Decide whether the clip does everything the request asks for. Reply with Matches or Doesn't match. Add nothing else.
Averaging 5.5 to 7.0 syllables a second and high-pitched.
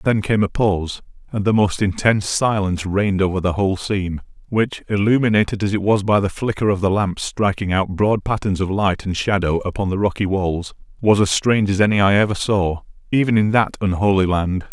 Doesn't match